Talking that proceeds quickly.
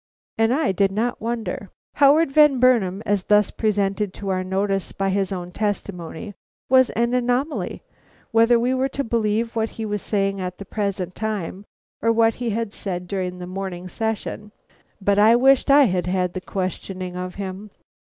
No: average, 175 wpm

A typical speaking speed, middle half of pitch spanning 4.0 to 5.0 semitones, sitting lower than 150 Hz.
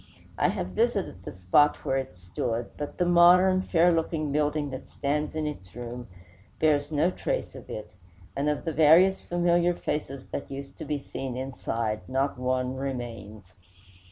Yes: average, 165 wpm; average, 4.4 semitones; medium, 140 Hz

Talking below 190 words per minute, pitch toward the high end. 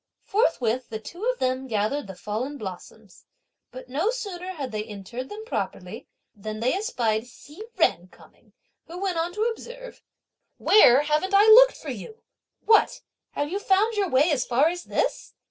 Yes: average, 170 wpm; very high, 295 Hz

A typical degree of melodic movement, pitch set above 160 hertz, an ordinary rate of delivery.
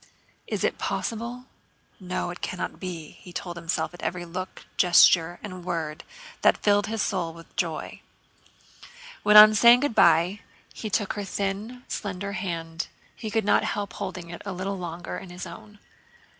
Yes: average, 3.1 semitones; medium, 185 Hz; average, 165 wpm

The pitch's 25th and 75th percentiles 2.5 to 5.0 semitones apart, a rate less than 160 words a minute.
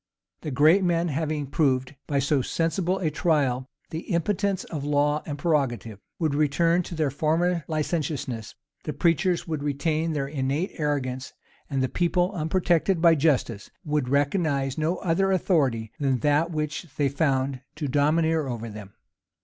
Yes: average, 3.4 semitones; average, 150 wpm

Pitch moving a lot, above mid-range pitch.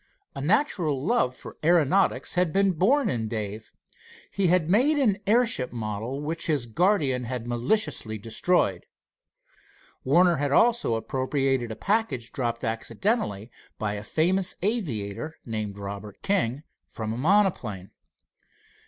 No: wide, 8.9 semitones; medium, 140 Hz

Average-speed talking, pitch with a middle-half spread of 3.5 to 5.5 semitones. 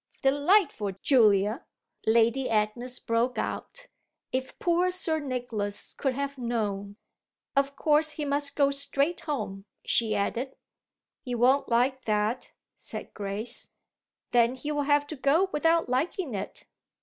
No: slow, 125 wpm; average, 4.4 semitones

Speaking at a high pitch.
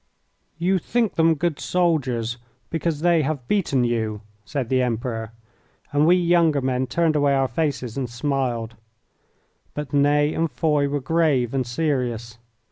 No: medium, 140 Hz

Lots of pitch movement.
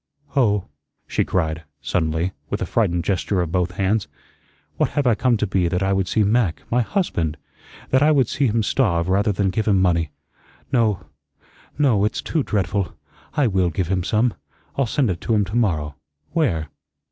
No: average, 4.7 semitones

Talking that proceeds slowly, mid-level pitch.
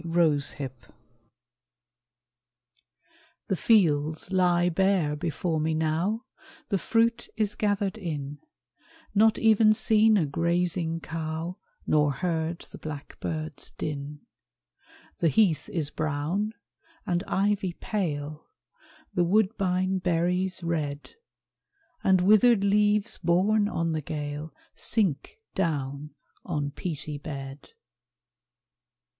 Yes: slow, 100 wpm; medium, 170 Hz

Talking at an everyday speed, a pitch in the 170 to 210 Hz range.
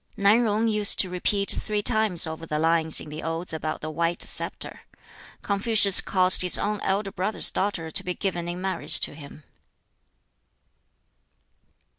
Yes: average, 155 wpm; medium, 185 Hz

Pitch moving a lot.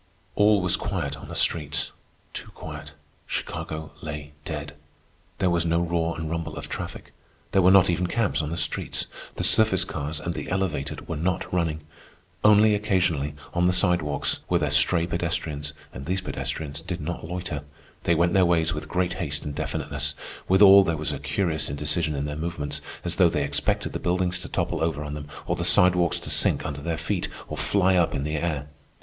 No: average, 3.2 semitones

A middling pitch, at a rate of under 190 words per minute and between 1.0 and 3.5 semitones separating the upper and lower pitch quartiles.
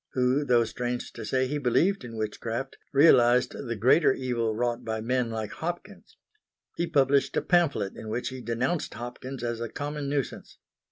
No: low, 125 Hz; average, 170 wpm; average, 3.2 semitones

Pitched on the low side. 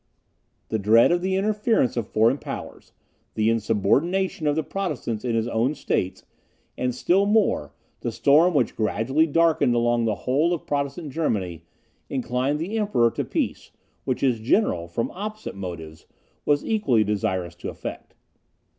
Yes: low, 125 Hz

